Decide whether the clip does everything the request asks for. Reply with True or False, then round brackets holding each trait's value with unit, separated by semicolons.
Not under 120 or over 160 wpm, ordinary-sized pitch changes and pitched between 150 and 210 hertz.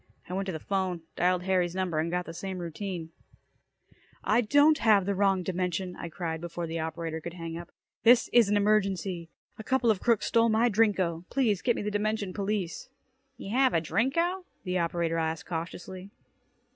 False (185 wpm; 4.0 semitones; 185 Hz)